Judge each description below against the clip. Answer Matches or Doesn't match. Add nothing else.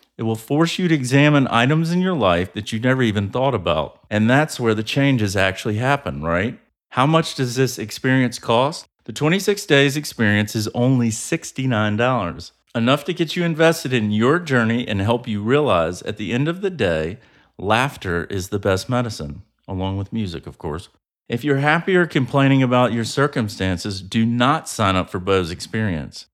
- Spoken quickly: Doesn't match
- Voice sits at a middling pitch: Doesn't match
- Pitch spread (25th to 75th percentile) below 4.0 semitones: Doesn't match